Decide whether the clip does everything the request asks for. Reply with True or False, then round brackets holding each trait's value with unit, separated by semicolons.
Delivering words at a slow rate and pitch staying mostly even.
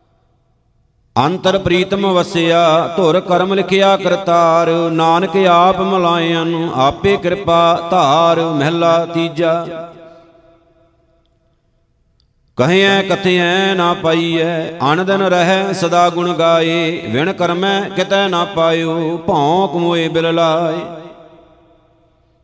True (85 wpm; 1.5 semitones)